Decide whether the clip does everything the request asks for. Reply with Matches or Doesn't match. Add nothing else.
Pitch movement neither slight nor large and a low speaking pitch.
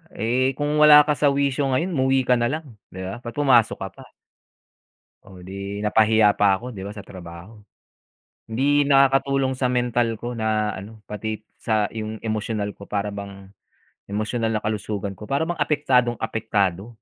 Matches